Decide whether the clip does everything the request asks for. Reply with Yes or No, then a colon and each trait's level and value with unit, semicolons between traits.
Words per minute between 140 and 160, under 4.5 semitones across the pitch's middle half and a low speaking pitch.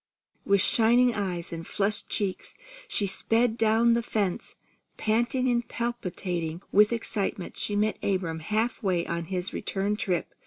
No: average, 145 wpm; average, 3.9 semitones; high, 205 Hz